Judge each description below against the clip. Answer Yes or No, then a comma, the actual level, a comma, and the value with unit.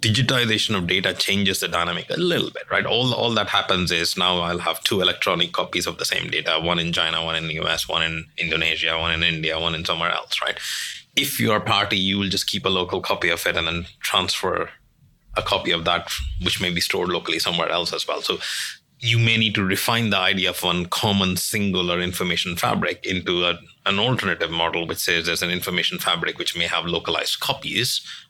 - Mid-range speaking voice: No, very low, 90 Hz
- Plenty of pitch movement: No, average, 2.7 semitones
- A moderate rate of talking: No, fast, 215 wpm